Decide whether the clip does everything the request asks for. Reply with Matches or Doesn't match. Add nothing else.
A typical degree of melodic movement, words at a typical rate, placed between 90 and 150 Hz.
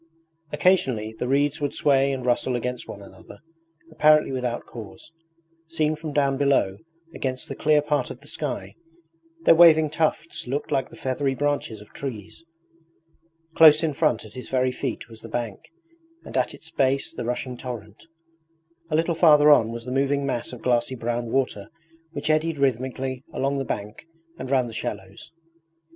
Matches